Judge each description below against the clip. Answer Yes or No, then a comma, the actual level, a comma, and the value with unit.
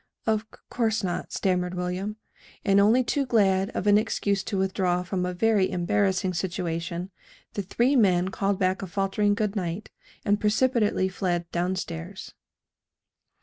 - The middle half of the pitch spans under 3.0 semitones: Yes, narrow, 2.5 semitones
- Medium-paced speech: Yes, average, 150 wpm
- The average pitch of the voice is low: No, high, 195 Hz